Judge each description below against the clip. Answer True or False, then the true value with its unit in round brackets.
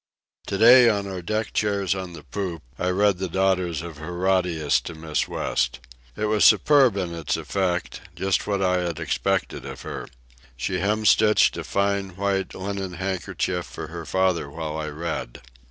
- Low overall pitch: True (95 Hz)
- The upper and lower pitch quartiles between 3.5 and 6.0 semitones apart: False (2.9 semitones)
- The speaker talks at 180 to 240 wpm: False (165 wpm)